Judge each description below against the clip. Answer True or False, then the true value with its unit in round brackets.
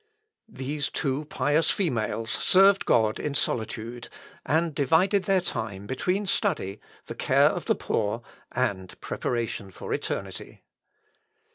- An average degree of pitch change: False (7.3 semitones)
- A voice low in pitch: True (130 Hz)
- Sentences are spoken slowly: True (120 wpm)